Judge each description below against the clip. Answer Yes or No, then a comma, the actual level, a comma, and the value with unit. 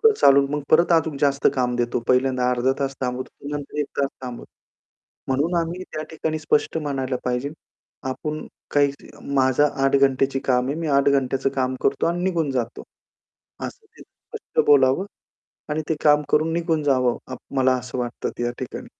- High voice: No, low, 135 Hz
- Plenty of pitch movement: No, average, 2.9 semitones